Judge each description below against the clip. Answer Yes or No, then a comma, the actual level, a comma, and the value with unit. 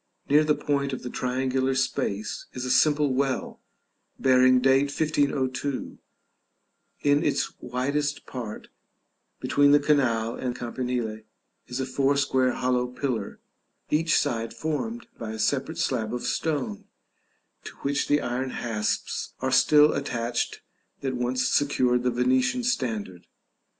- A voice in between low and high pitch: No, low, 130 Hz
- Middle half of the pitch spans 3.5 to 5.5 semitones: No, narrow, 2.5 semitones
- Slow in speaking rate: Yes, slow, 130 wpm